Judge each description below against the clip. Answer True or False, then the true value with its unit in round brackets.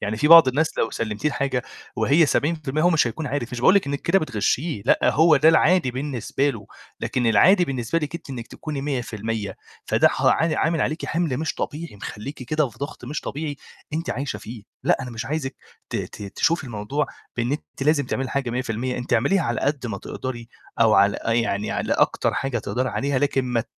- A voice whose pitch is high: False (135 Hz)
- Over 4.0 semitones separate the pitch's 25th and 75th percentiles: True (4.5 semitones)